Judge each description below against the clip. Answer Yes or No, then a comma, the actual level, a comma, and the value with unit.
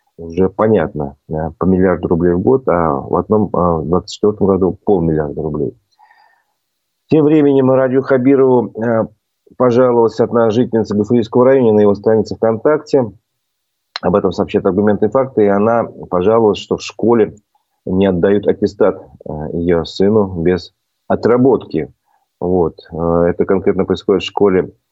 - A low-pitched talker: Yes, low, 105 Hz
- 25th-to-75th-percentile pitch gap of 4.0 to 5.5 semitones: Yes, average, 5.2 semitones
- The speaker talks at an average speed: Yes, average, 130 wpm